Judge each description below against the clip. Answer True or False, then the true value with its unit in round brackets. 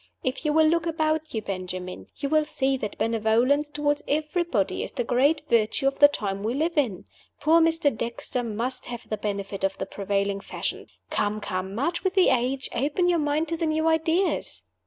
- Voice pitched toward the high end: True (270 Hz)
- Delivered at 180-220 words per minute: True (195 wpm)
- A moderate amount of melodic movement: False (6.5 semitones)